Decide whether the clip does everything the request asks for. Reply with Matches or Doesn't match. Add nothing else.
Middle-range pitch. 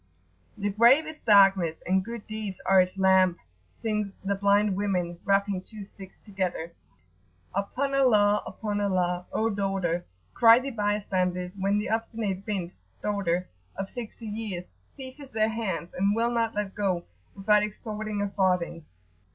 Doesn't match